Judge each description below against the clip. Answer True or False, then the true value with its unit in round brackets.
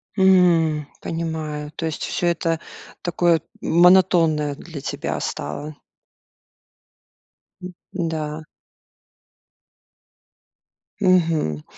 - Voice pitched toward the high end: False (165 Hz)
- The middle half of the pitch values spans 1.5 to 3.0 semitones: True (2.4 semitones)